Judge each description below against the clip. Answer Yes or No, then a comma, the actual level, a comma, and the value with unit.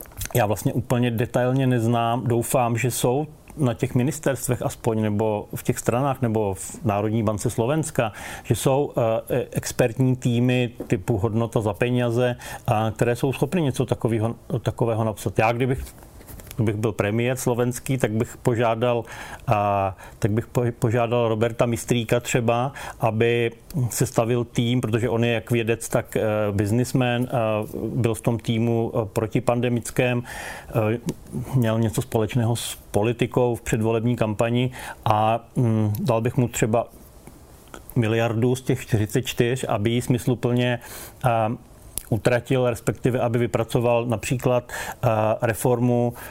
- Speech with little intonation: Yes, narrow, 1.8 semitones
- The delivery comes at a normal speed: Yes, average, 120 wpm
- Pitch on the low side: Yes, low, 120 Hz